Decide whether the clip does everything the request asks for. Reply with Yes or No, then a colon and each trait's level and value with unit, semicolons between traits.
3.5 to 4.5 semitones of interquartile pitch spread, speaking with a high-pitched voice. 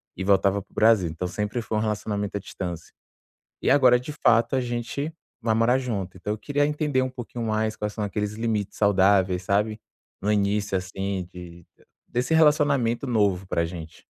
No: average, 3.8 semitones; low, 105 Hz